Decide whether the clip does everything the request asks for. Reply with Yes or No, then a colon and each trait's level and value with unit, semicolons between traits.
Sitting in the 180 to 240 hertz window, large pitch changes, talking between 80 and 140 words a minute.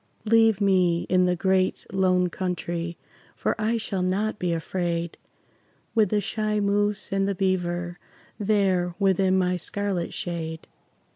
No: medium, 185 Hz; narrow, 2.5 semitones; slow, 135 wpm